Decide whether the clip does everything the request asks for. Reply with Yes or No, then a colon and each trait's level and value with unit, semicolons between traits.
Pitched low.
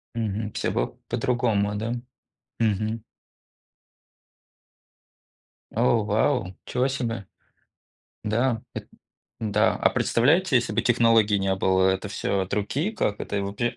Yes: low, 110 Hz